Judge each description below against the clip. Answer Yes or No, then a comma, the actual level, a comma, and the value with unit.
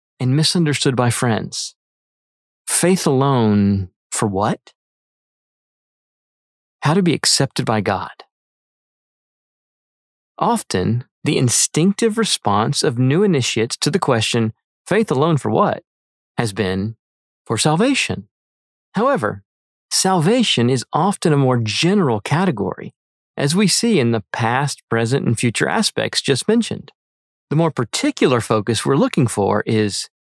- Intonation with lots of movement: Yes, wide, 7.3 semitones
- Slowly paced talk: Yes, slow, 120 wpm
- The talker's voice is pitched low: Yes, low, 125 Hz